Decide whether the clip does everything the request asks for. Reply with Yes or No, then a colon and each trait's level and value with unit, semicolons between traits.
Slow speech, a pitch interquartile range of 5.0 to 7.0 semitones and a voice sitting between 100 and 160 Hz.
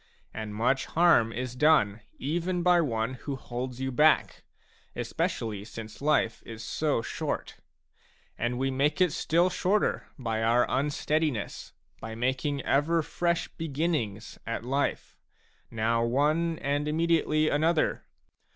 Yes: slow, 130 wpm; average, 5.3 semitones; low, 135 Hz